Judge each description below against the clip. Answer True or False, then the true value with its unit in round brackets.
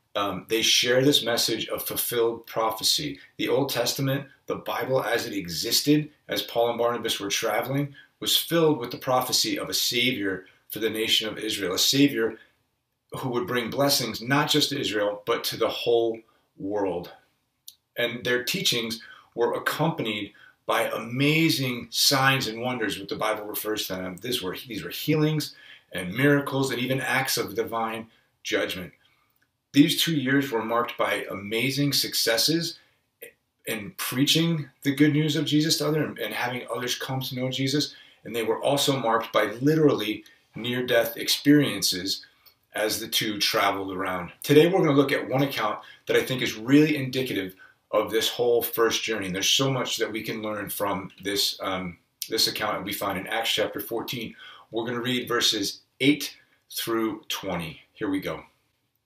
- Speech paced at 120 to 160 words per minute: False (170 wpm)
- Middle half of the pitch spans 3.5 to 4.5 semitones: True (4.2 semitones)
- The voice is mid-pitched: False (120 Hz)